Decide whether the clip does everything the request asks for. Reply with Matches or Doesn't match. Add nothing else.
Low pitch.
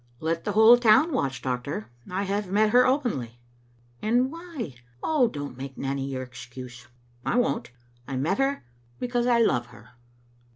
Doesn't match